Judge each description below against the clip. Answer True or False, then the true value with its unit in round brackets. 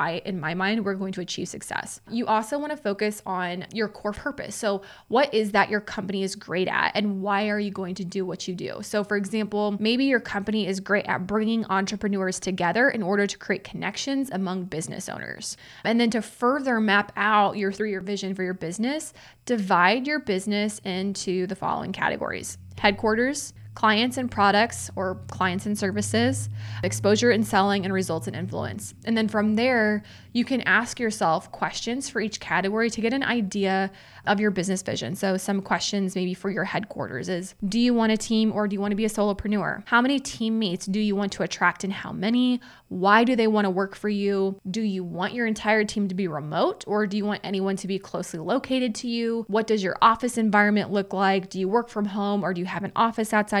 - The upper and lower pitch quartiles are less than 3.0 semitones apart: True (2.6 semitones)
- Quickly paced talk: True (215 wpm)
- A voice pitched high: True (205 Hz)